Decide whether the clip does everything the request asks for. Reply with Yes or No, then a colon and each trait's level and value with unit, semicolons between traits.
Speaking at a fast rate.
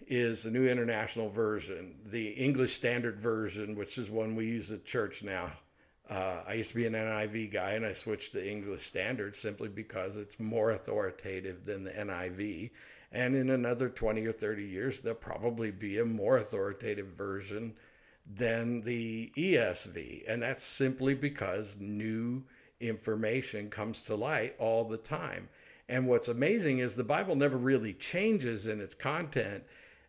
No: average, 160 wpm